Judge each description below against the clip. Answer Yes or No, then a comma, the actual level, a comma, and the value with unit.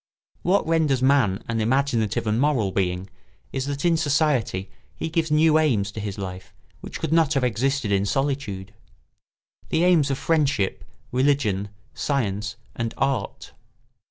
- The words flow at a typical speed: Yes, average, 145 wpm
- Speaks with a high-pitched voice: No, low, 135 Hz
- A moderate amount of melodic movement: No, wide, 6.2 semitones